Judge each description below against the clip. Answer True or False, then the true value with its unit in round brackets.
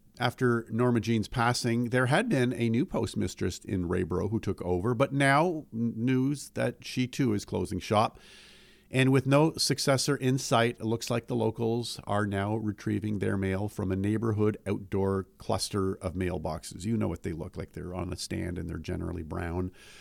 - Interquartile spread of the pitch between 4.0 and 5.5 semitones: True (4.6 semitones)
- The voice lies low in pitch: True (110 Hz)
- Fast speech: False (185 wpm)